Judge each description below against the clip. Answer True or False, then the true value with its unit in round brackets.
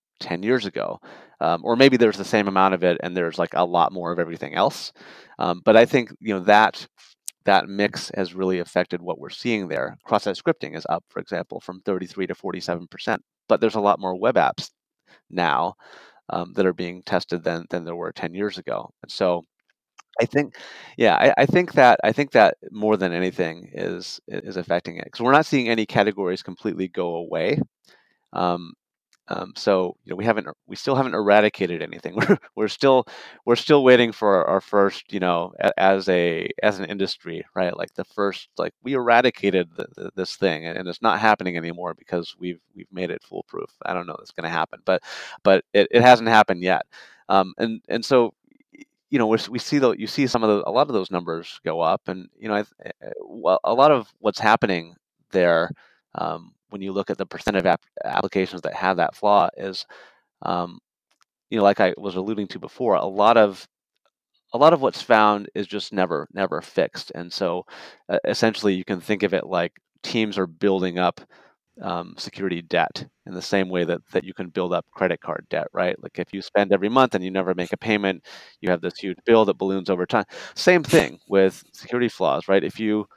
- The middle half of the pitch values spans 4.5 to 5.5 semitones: False (3.6 semitones)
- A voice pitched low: True (95 Hz)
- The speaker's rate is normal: False (210 wpm)